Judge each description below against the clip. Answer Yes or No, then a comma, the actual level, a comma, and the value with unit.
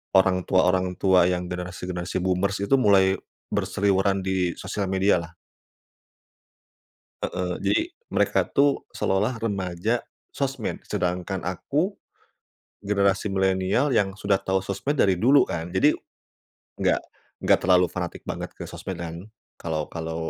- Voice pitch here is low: Yes, very low, 95 Hz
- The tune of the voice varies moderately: No, narrow, 1.8 semitones